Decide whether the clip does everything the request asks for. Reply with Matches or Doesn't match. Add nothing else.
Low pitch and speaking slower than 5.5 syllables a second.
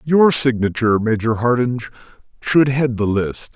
Matches